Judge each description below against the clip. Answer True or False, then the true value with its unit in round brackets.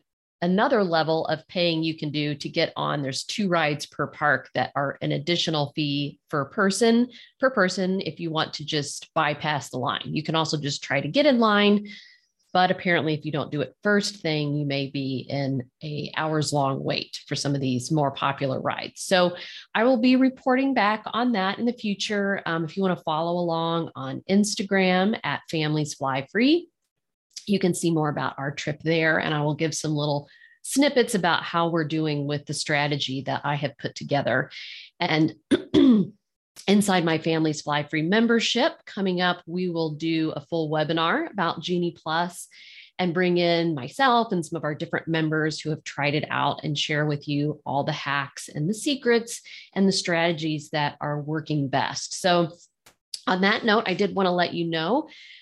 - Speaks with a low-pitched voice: False (165 Hz)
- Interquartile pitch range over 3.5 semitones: True (4.6 semitones)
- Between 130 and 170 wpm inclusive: False (190 wpm)